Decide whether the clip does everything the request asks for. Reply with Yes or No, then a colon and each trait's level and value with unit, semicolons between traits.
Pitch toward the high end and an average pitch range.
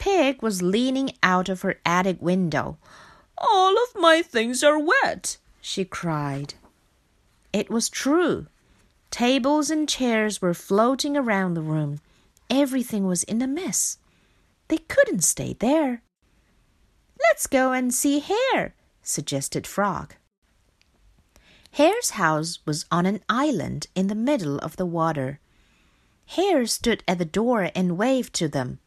No: high, 215 Hz; wide, 9.0 semitones